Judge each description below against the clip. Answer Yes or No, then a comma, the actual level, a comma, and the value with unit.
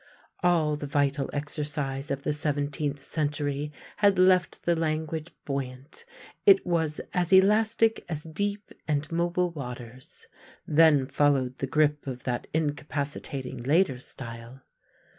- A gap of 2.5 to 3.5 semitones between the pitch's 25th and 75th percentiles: Yes, average, 3.2 semitones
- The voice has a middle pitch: Yes, medium, 150 Hz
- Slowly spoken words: Yes, slow, 125 wpm